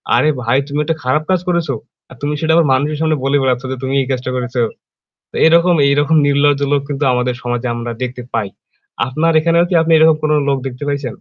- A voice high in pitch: No, medium, 140 Hz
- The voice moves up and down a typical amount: Yes, average, 3.7 semitones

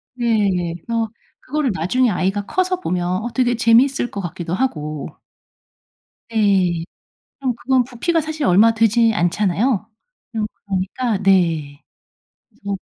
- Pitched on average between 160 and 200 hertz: No, high, 215 Hz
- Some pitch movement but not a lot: Yes, average, 5.0 semitones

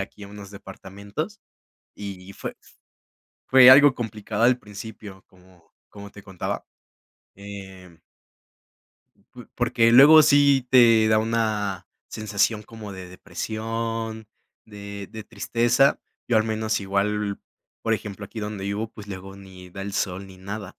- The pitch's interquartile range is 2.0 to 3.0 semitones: Yes, narrow, 2.5 semitones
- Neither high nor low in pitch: No, low, 105 Hz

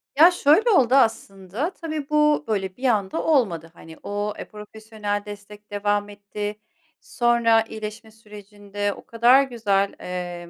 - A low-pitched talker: No, high, 210 Hz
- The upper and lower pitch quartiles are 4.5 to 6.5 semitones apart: No, average, 2.9 semitones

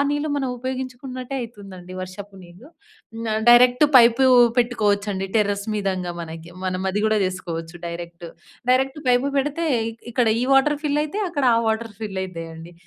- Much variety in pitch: Yes, wide, 5.7 semitones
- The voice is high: Yes, high, 220 Hz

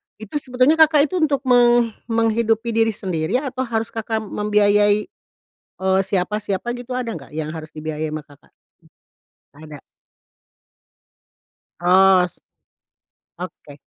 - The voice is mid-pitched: No, high, 210 Hz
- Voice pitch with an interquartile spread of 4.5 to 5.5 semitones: Yes, average, 5.1 semitones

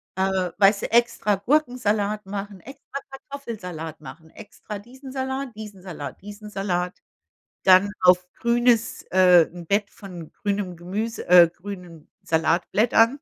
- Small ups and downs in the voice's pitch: No, average, 4.1 semitones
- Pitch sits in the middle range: No, high, 200 Hz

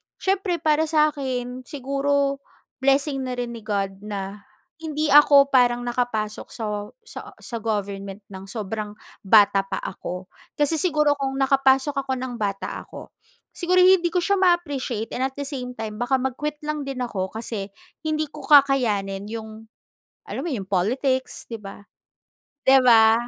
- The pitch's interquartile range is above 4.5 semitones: Yes, average, 5.1 semitones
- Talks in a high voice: Yes, very high, 255 Hz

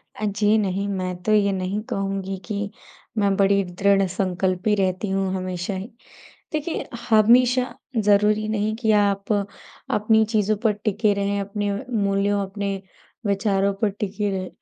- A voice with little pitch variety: Yes, narrow, 1.5 semitones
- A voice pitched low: No, high, 200 Hz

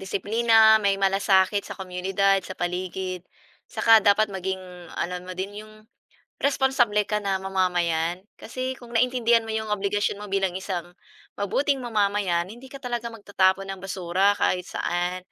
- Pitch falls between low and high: No, high, 195 Hz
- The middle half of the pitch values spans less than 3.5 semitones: Yes, average, 2.8 semitones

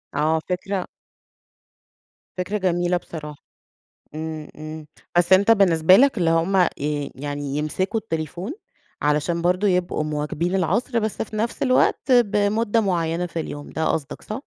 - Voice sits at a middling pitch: Yes, medium, 175 Hz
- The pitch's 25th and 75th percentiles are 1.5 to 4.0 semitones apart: No, average, 4.5 semitones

